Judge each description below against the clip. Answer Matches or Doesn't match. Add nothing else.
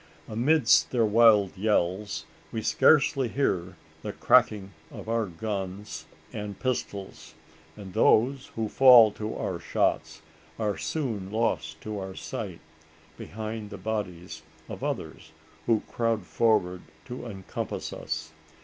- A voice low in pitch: Matches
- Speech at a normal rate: Doesn't match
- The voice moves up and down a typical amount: Matches